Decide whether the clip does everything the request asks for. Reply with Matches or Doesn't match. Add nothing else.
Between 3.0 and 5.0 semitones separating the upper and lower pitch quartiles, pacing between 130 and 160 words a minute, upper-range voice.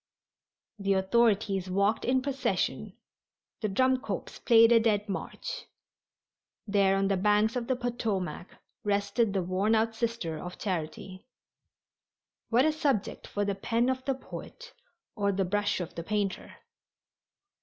Matches